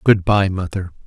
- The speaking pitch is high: No, very low, 95 Hz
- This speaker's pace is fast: No, average, 170 wpm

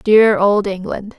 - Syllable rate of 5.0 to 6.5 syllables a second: No, 3.5 syllables/s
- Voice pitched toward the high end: Yes, high, 205 Hz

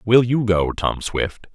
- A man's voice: Yes, male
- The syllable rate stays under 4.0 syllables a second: Yes, 3.7 syllables/s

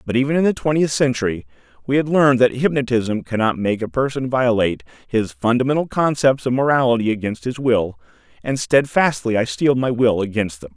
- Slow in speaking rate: No, average, 180 wpm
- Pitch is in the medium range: No, low, 120 Hz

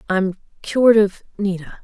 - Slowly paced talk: Yes, slow, 100 wpm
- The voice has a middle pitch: No, high, 200 Hz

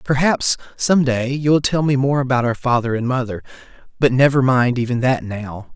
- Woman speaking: No, male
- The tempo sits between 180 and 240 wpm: No, average, 155 wpm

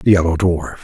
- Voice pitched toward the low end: Yes, very low, 85 Hz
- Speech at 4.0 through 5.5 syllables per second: No, 6.0 syllables/s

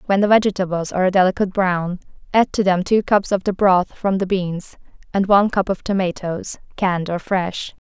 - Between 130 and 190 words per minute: No, average, 200 wpm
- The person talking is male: No, female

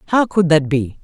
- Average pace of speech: No, fast, 230 wpm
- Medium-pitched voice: Yes, medium, 165 Hz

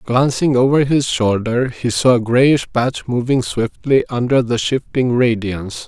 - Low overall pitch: Yes, low, 125 Hz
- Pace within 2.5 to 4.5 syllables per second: Yes, 4.2 syllables/s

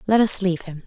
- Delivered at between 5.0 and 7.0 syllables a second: Yes, 6.9 syllables/s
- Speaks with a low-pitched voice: No, high, 190 Hz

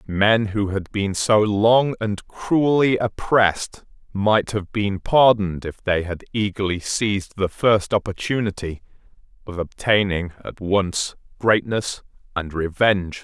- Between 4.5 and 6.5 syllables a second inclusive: No, 3.9 syllables/s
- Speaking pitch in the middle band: No, low, 100 Hz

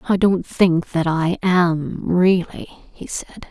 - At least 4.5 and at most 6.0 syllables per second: No, 3.1 syllables/s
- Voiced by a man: No, female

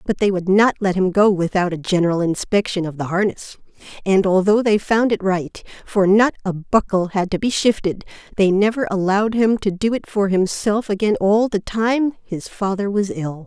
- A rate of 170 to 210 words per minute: Yes, average, 200 wpm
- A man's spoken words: No, female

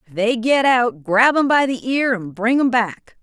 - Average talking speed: No, fast, 240 wpm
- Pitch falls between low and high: No, high, 235 Hz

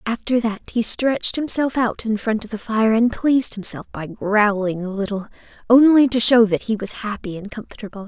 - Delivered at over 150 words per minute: Yes, average, 200 wpm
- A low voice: No, high, 220 Hz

